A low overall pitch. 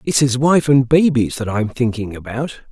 Yes: low, 125 Hz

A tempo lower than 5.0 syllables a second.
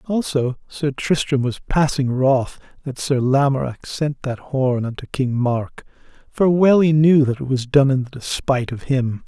Yes: 4.4 syllables/s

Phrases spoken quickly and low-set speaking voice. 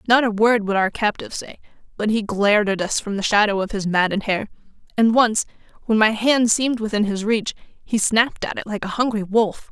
No: fast, 220 wpm; high, 215 Hz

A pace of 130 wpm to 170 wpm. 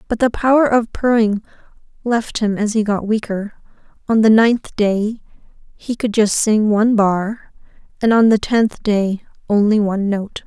Yes: average, 165 wpm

